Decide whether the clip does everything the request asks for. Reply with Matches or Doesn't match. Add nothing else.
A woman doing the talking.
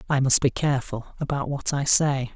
Doesn't match